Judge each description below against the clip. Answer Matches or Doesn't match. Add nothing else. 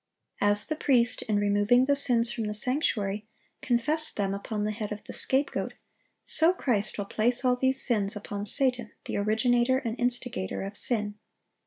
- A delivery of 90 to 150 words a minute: Doesn't match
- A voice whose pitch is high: Matches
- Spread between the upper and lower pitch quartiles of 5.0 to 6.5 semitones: Doesn't match